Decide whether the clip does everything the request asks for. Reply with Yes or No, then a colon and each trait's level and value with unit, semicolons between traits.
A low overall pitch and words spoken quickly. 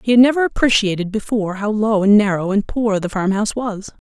No: high, 210 Hz; fast, 220 wpm